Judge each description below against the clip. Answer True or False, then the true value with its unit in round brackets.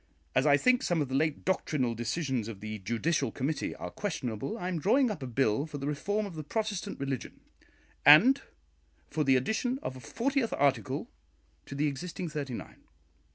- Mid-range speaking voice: True (145 Hz)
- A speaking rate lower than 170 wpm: False (185 wpm)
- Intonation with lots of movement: True (6.0 semitones)